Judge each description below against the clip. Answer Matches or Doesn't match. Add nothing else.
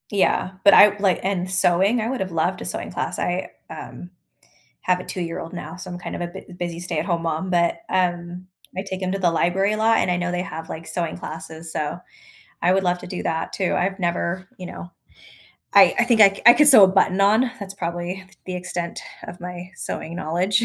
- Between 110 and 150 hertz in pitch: Doesn't match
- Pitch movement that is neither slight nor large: Doesn't match